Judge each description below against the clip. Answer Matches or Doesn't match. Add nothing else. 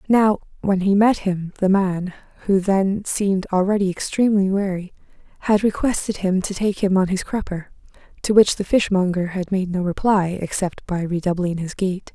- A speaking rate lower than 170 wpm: Doesn't match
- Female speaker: Matches